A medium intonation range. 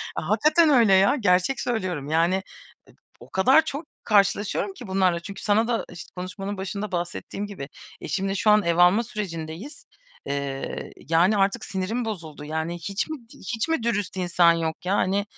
Yes: average, 3.7 semitones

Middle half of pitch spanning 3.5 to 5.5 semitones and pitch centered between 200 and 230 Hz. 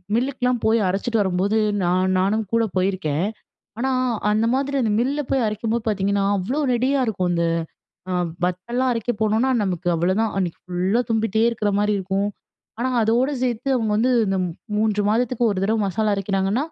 Yes: average, 3.8 semitones; high, 215 Hz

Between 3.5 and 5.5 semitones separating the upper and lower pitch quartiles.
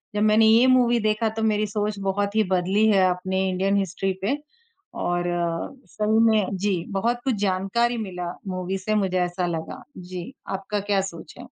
No: narrow, 2.6 semitones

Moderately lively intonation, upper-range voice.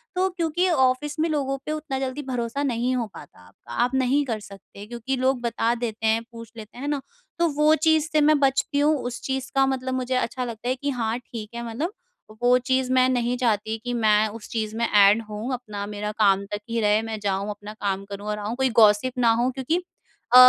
Yes: average, 3.8 semitones; high, 245 Hz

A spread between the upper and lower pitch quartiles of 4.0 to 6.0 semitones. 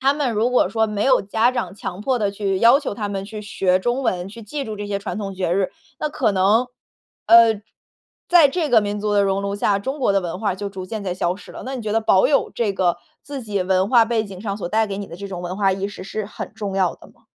No: average, 3.0 semitones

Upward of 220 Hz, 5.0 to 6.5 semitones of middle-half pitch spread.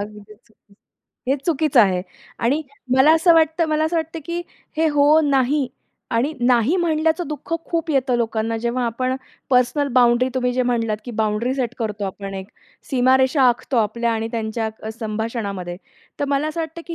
Yes: very high, 250 Hz; average, 5.3 semitones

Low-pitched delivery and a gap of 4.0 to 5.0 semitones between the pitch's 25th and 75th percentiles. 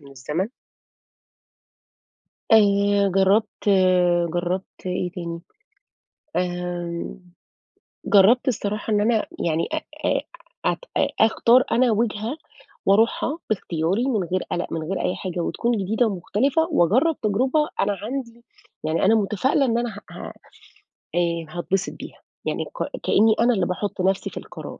No: high, 200 Hz; average, 4.5 semitones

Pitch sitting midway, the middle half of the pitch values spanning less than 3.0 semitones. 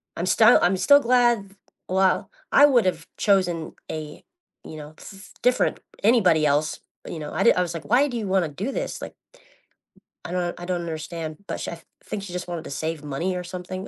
No: medium, 180 Hz; average, 3.8 semitones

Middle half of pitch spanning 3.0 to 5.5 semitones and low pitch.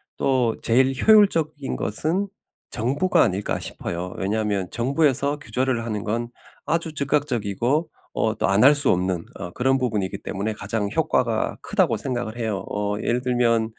Yes: average, 5.2 semitones; low, 120 Hz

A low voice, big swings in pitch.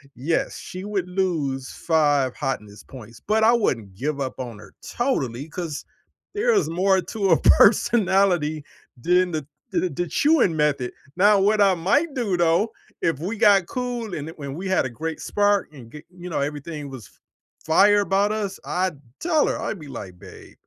No: medium, 175 Hz; wide, 5.9 semitones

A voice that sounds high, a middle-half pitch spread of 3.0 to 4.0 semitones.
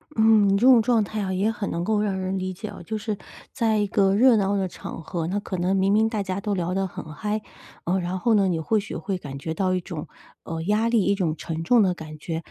Yes: high, 195 Hz; average, 3.3 semitones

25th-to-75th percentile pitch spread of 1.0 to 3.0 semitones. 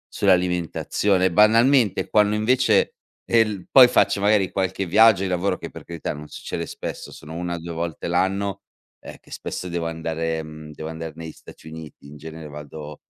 No: average, 3.9 semitones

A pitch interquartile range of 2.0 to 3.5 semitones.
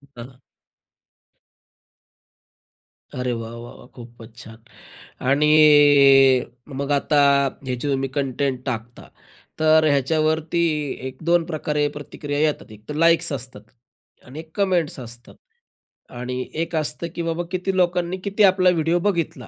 No: average, 4.8 semitones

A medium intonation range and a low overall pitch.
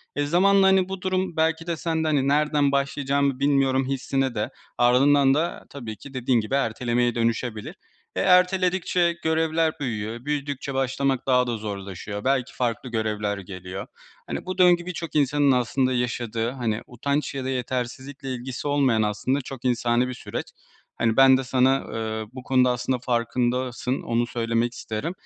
Yes: average, 3.4 semitones; low, 130 Hz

